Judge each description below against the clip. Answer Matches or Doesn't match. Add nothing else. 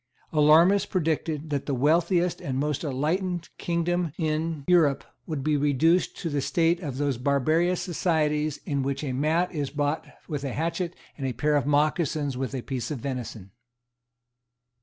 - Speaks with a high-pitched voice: Doesn't match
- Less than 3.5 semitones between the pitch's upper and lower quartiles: Matches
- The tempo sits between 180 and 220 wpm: Doesn't match